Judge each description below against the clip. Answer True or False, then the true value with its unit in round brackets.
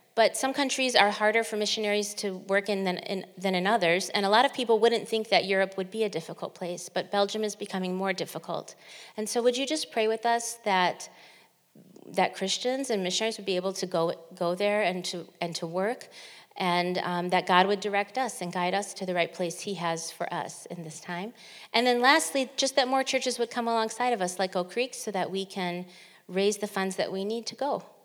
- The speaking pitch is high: True (200 Hz)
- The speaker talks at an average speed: False (230 wpm)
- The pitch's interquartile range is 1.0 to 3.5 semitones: False (4.0 semitones)